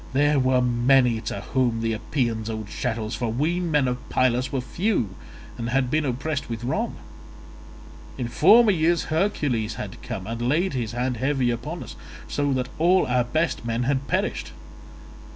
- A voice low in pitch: Yes, low, 130 Hz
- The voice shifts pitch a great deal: No, average, 4.0 semitones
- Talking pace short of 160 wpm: No, average, 170 wpm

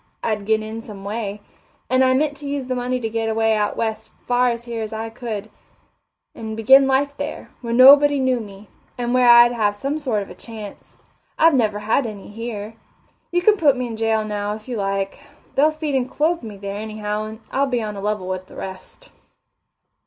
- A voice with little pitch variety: No, average, 3.5 semitones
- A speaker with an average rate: No, fast, 215 wpm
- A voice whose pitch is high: Yes, high, 225 Hz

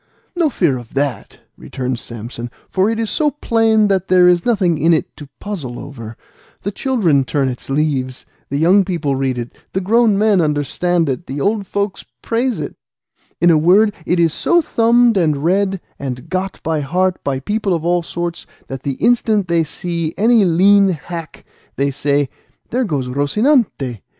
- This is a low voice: No, medium, 175 Hz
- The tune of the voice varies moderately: No, wide, 6.5 semitones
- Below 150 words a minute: No, average, 175 wpm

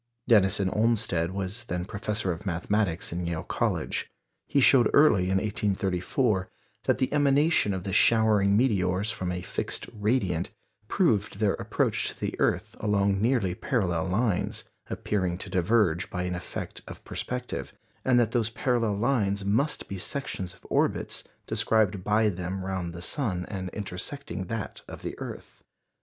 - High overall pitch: No, low, 100 Hz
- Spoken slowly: No, average, 150 wpm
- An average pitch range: Yes, average, 3.7 semitones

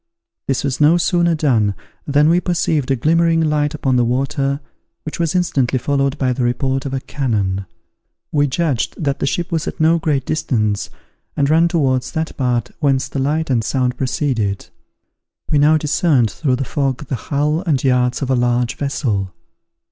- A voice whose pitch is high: No, medium, 140 Hz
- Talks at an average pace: Yes, average, 180 wpm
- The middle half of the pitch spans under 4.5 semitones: Yes, average, 3.5 semitones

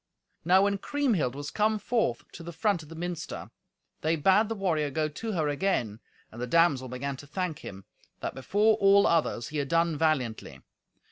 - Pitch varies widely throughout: Yes, wide, 5.7 semitones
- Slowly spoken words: No, average, 190 wpm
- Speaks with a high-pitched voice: No, medium, 165 Hz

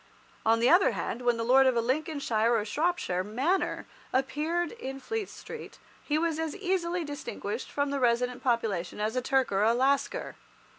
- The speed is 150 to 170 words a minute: No, average, 180 wpm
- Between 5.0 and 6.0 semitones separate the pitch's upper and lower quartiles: Yes, wide, 5.6 semitones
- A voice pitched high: Yes, very high, 265 Hz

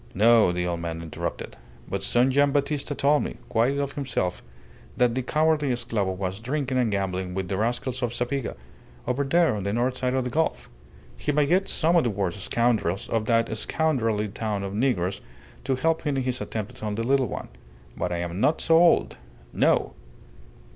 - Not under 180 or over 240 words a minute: Yes, average, 195 wpm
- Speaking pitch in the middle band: No, low, 120 Hz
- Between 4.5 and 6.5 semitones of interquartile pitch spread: Yes, wide, 5.6 semitones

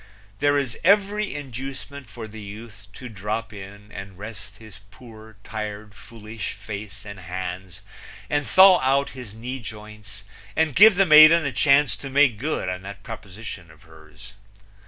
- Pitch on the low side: Yes, low, 110 Hz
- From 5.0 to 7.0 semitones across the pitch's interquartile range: Yes, average, 5.3 semitones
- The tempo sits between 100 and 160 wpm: Yes, average, 155 wpm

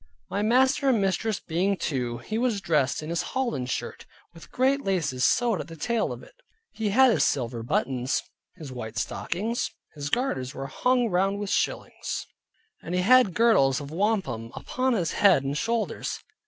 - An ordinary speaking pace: Yes, average, 175 wpm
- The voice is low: No, high, 190 Hz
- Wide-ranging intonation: Yes, wide, 9.0 semitones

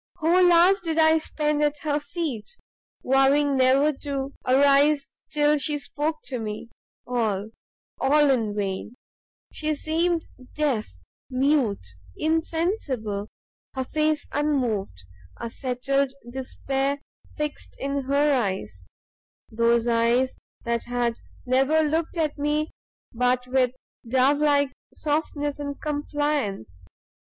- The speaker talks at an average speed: No, slow, 110 wpm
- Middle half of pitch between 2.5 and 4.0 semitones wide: Yes, average, 3.6 semitones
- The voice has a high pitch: Yes, very high, 280 Hz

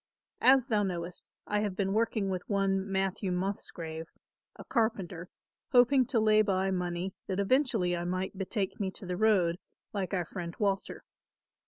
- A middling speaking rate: Yes, average, 160 wpm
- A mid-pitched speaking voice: No, high, 195 Hz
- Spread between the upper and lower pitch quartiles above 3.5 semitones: No, average, 3.0 semitones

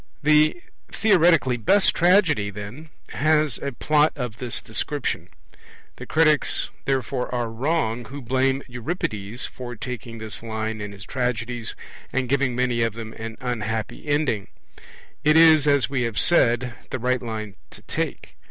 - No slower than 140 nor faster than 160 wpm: Yes, average, 145 wpm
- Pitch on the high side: No, low, 125 Hz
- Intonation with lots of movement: No, average, 4.7 semitones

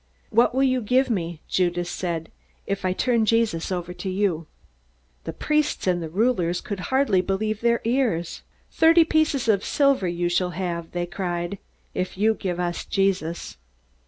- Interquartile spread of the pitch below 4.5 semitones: No, average, 5.1 semitones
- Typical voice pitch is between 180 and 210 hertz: Yes, high, 190 Hz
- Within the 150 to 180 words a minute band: Yes, average, 160 wpm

